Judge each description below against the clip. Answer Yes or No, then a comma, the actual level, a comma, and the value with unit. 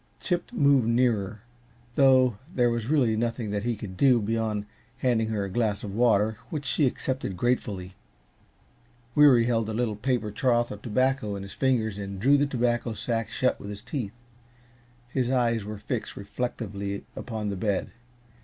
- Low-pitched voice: Yes, low, 115 Hz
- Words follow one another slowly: No, average, 165 wpm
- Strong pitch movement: No, average, 3.4 semitones